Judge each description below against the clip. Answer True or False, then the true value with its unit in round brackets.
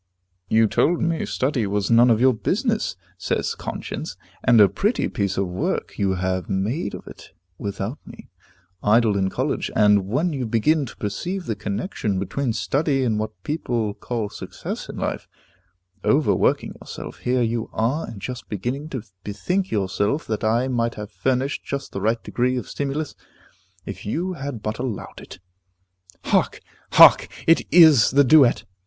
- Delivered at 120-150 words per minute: False (160 wpm)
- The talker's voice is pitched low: True (120 Hz)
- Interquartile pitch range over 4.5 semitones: True (5.2 semitones)